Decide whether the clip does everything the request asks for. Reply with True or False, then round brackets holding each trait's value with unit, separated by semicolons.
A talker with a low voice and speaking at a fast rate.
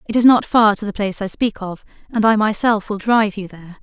False (210 Hz; 265 wpm)